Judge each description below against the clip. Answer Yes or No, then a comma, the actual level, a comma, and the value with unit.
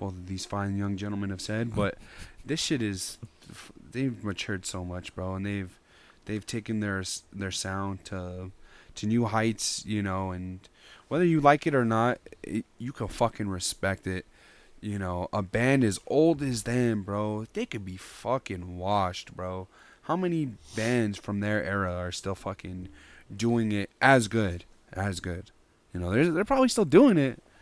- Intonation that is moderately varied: Yes, average, 3.6 semitones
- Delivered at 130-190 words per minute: Yes, average, 170 wpm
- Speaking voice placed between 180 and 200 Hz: No, low, 100 Hz